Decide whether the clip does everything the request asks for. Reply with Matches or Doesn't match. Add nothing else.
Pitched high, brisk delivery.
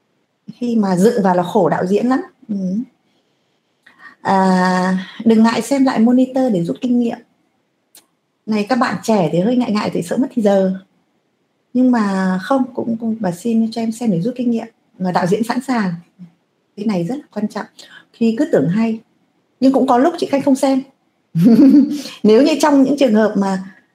Doesn't match